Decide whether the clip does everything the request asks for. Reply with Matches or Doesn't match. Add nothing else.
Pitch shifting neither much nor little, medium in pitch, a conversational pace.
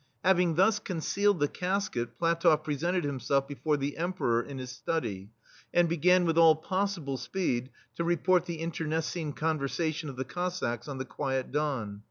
Matches